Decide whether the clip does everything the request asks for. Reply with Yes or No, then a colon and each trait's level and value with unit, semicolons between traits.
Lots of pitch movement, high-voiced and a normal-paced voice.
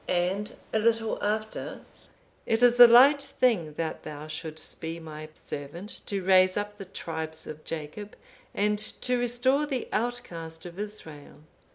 Yes: wide, 6.0 semitones; high, 195 Hz; average, 155 wpm